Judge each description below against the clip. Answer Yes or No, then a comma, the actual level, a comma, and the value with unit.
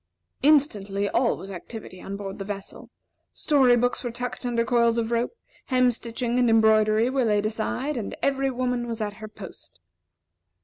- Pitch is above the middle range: Yes, high, 235 Hz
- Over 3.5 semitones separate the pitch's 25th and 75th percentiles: No, average, 2.7 semitones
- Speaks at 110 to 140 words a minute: No, average, 170 wpm